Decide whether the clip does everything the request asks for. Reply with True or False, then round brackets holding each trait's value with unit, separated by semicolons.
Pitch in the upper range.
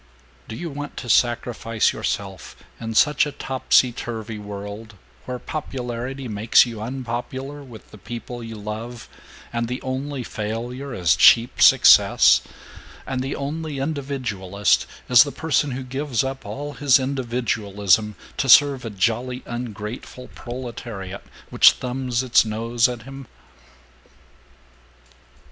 False (120 Hz)